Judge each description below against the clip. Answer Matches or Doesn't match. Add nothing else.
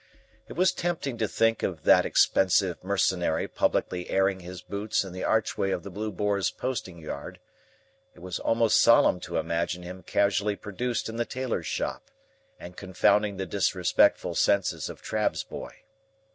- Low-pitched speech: Matches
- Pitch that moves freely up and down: Doesn't match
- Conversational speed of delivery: Matches